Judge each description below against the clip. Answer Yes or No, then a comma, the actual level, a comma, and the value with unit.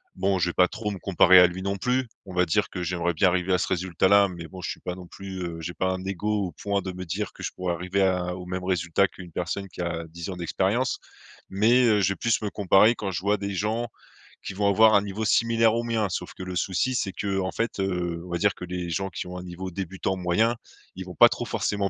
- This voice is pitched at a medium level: No, very low, 95 Hz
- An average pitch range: No, narrow, 2.2 semitones